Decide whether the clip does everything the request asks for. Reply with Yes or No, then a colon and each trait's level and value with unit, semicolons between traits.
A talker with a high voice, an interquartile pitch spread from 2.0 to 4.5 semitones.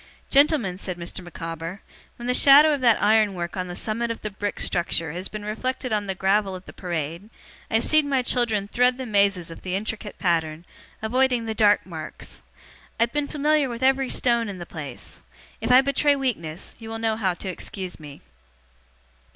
No: high, 210 Hz; wide, 5.5 semitones